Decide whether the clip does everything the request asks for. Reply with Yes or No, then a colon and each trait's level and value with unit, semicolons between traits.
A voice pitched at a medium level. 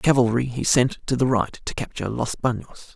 No: low, 120 Hz